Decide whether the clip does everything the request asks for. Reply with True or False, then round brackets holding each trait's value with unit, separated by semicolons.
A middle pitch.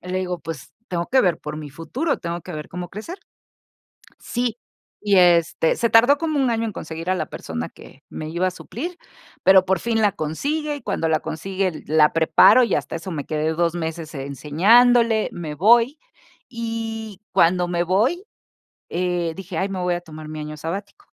True (180 Hz)